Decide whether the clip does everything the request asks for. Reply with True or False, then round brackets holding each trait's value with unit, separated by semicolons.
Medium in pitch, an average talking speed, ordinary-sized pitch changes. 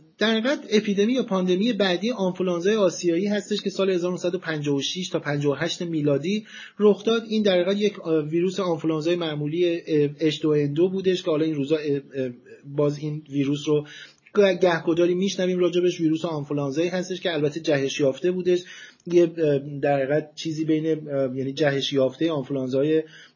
True (165 Hz; 140 wpm; 3.9 semitones)